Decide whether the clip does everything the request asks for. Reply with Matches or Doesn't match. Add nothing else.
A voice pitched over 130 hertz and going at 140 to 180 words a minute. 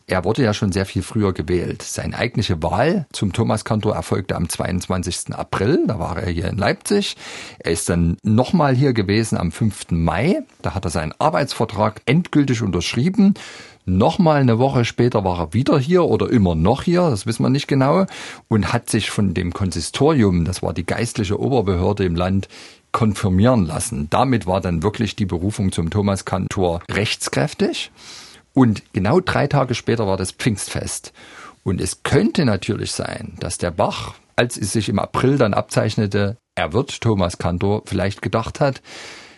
Doesn't match